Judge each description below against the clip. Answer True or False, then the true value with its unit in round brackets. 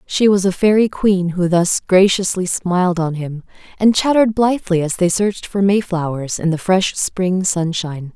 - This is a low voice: False (185 Hz)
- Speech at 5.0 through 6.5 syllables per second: False (4.8 syllables/s)